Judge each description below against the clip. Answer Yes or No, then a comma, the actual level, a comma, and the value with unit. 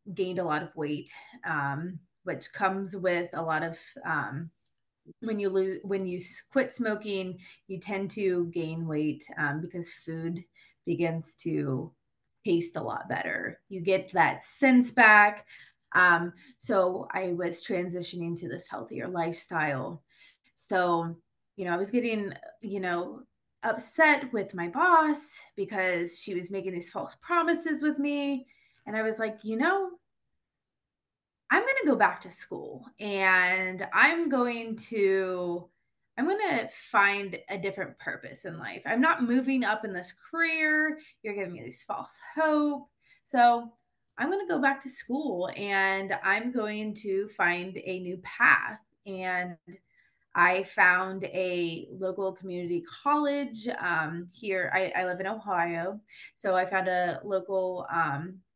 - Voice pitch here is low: No, high, 190 Hz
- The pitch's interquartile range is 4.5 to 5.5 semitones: Yes, average, 5.1 semitones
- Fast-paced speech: No, average, 145 wpm